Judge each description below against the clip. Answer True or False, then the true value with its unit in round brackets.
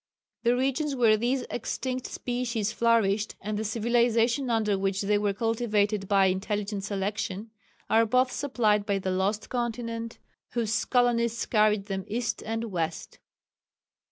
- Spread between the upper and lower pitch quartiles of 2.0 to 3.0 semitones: True (2.7 semitones)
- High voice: True (220 Hz)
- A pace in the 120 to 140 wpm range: True (135 wpm)